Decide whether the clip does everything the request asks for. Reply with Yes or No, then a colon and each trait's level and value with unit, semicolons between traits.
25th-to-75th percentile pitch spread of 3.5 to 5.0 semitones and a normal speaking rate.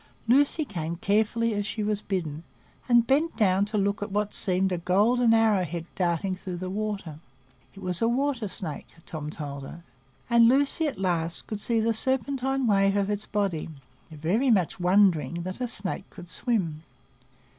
Yes: average, 4.4 semitones; average, 175 wpm